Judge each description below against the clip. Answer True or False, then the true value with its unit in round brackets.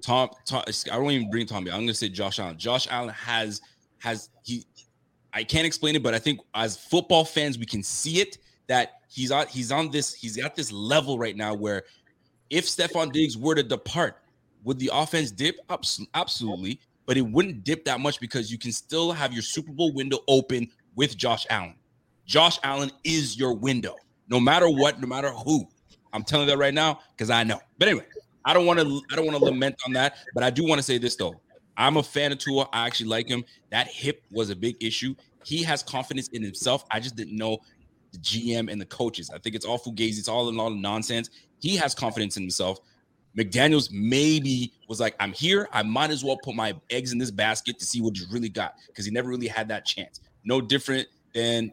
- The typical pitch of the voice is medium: False (125 Hz)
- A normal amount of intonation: True (4.5 semitones)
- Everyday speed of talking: False (225 wpm)